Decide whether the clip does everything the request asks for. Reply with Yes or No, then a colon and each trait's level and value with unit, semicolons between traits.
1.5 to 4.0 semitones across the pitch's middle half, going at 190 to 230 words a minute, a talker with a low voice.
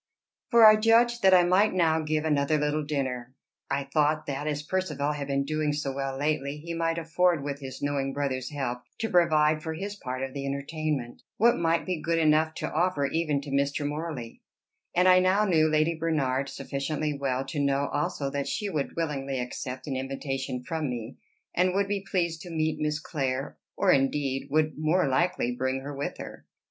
No: average, 3.3 semitones; average, 195 wpm; medium, 150 Hz